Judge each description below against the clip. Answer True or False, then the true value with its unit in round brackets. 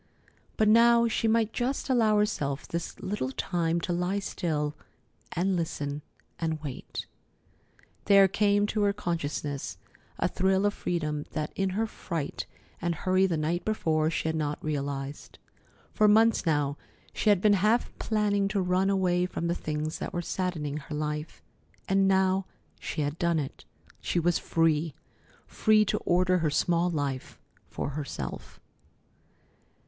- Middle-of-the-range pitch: True (175 Hz)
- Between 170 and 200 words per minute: False (150 wpm)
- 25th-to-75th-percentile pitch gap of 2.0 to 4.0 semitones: False (4.7 semitones)